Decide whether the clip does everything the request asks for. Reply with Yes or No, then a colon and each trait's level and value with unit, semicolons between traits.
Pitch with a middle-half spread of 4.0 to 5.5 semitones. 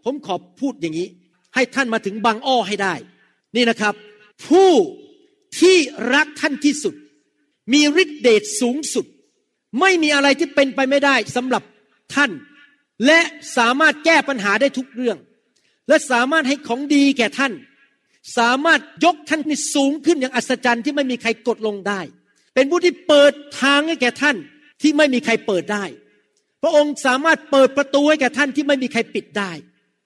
Yes: average, 4.4 semitones